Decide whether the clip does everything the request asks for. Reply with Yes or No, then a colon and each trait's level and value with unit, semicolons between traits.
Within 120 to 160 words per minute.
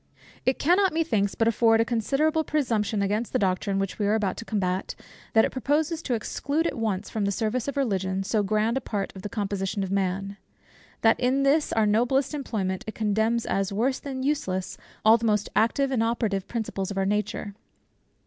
No: average, 195 wpm